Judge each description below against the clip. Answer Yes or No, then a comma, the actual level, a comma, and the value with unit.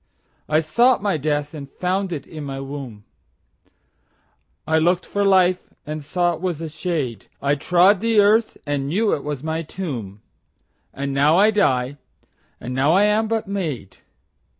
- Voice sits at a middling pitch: Yes, medium, 160 Hz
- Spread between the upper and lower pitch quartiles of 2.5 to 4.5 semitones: No, average, 5.3 semitones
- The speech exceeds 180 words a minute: No, average, 150 wpm